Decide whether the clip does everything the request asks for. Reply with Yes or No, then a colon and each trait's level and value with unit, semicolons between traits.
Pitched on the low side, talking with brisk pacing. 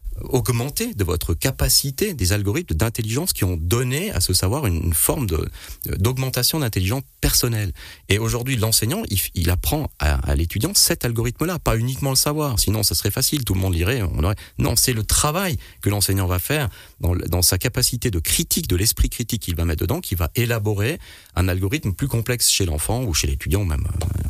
No: low, 100 Hz; average, 195 wpm